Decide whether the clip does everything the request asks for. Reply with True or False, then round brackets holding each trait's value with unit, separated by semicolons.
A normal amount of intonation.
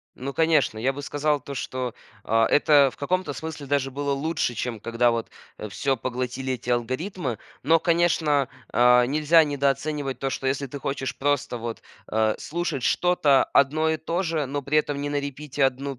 True (3.0 semitones)